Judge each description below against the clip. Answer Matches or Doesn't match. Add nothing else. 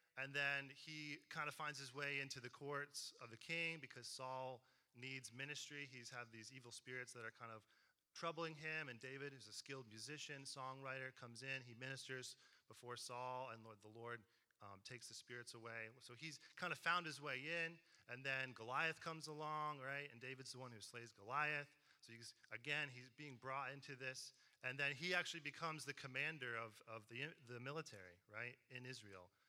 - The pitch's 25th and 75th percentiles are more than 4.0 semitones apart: Doesn't match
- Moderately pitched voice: Doesn't match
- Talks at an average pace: Matches